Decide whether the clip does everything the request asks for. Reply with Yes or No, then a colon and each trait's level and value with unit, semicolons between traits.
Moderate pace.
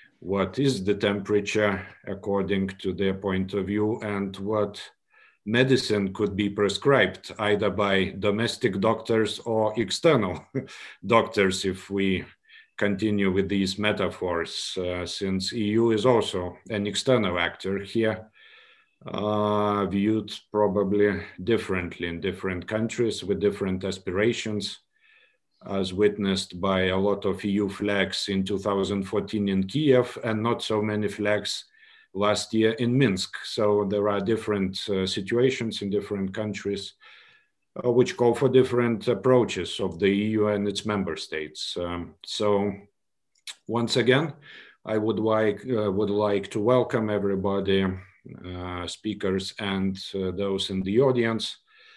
No: slow, 130 wpm